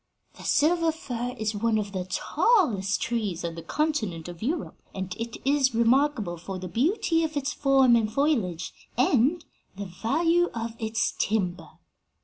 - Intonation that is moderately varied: No, wide, 7.0 semitones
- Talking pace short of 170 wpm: Yes, average, 155 wpm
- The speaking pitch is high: Yes, high, 230 Hz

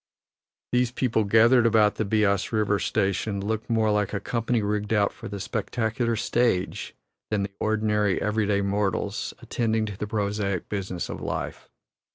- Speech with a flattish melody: Yes, narrow, 1.9 semitones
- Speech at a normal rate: Yes, average, 150 wpm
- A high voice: No, low, 105 Hz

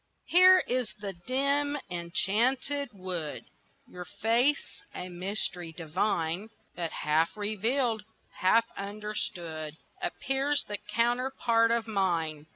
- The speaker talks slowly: Yes, slow, 100 wpm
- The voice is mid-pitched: No, high, 210 Hz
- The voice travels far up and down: Yes, wide, 6.1 semitones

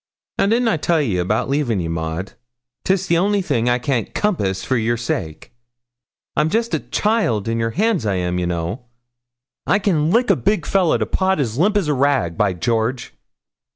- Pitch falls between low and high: No, low, 130 Hz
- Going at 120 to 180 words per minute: No, average, 195 wpm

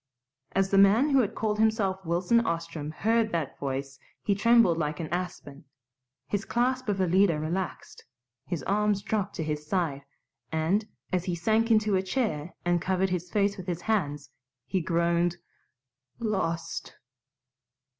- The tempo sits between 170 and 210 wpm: No, average, 150 wpm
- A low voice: No, medium, 185 Hz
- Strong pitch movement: No, average, 4.1 semitones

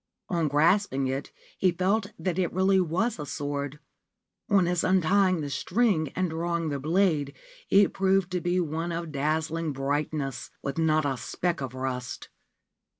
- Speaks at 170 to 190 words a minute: No, average, 160 wpm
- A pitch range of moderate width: Yes, average, 4.2 semitones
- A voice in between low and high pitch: Yes, medium, 165 Hz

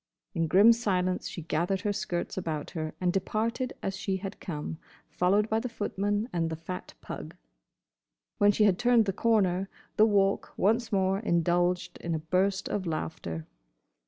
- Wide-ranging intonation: No, average, 3.2 semitones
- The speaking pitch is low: No, high, 190 Hz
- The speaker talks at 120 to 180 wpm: Yes, average, 165 wpm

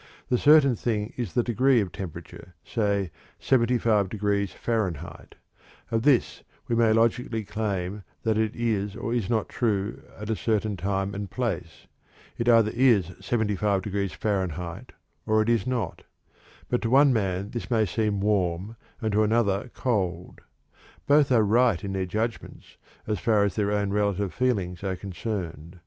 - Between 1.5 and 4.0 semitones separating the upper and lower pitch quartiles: Yes, average, 3.1 semitones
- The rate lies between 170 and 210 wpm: No, average, 160 wpm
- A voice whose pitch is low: Yes, low, 105 Hz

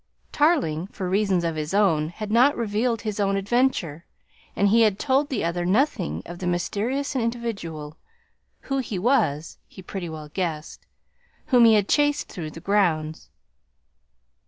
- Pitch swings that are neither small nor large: No, wide, 5.9 semitones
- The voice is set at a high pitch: Yes, high, 200 Hz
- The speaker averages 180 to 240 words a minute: No, average, 155 wpm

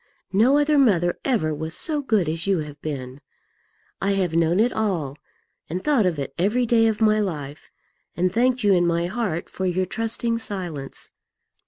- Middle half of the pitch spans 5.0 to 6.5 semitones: Yes, wide, 5.6 semitones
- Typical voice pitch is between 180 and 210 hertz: Yes, high, 190 Hz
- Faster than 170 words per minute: Yes, average, 180 wpm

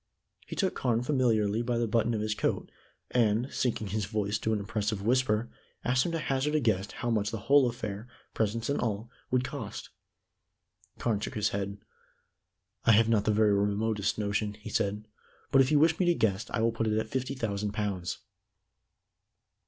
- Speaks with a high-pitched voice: No, low, 110 Hz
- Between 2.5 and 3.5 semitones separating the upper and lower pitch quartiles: Yes, average, 3.0 semitones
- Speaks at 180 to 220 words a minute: Yes, average, 190 wpm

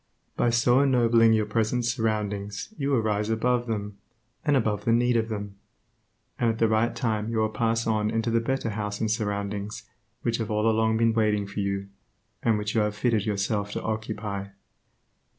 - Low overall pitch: Yes, low, 110 Hz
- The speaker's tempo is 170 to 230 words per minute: Yes, average, 185 wpm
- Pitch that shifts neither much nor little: No, narrow, 1.7 semitones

